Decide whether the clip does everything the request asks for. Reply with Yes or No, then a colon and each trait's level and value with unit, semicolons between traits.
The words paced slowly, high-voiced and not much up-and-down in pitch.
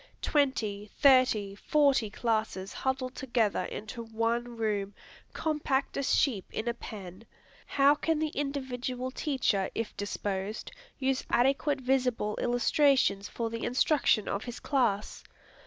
No: slow, 125 wpm; high, 240 Hz; average, 4.0 semitones